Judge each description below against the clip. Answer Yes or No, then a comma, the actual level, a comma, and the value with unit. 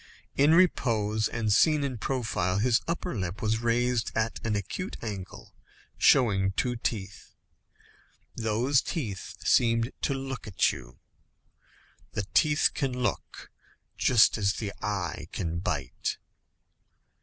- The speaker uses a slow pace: Yes, slow, 120 wpm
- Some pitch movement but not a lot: Yes, average, 4.2 semitones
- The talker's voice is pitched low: Yes, low, 115 Hz